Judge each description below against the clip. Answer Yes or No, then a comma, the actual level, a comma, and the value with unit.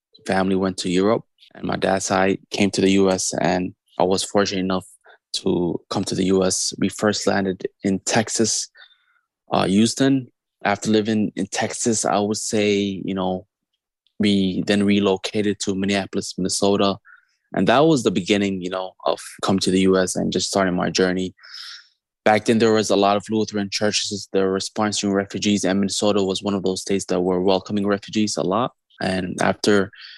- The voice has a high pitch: No, low, 100 Hz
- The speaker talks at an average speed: Yes, average, 175 wpm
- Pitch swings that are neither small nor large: No, narrow, 1.6 semitones